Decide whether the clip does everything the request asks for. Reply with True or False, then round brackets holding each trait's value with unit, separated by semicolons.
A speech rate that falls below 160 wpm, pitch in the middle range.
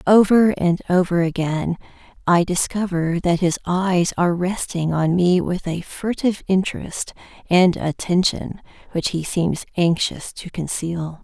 True (135 wpm; 175 Hz)